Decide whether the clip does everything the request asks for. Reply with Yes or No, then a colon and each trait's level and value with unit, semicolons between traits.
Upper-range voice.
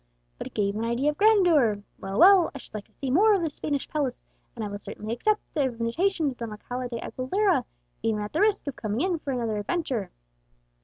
Yes: very high, 260 Hz